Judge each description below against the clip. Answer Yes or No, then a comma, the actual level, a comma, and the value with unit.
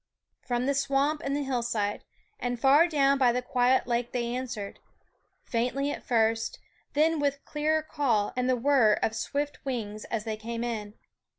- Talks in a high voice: Yes, very high, 250 Hz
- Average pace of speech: Yes, average, 170 wpm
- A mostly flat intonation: No, average, 3.4 semitones